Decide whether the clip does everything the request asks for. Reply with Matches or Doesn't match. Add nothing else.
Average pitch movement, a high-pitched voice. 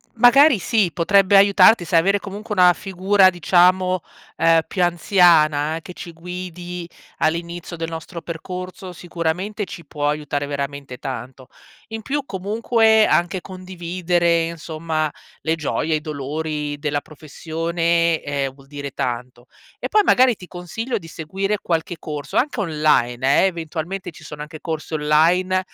Doesn't match